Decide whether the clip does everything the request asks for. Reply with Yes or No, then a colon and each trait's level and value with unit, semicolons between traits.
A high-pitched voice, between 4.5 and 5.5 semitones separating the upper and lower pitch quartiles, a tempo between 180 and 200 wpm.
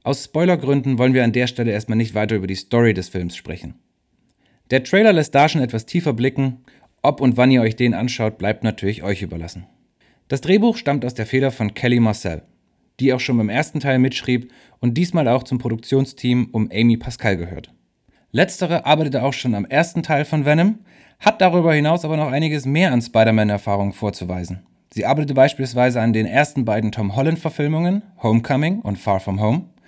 No: low, 125 Hz; average, 5.0 semitones; average, 185 wpm